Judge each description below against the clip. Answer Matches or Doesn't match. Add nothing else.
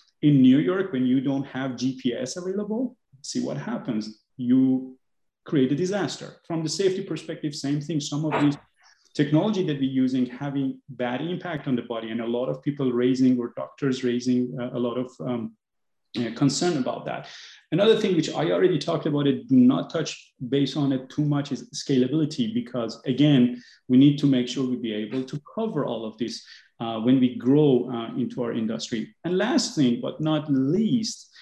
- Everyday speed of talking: Matches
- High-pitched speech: Doesn't match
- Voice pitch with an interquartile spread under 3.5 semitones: Doesn't match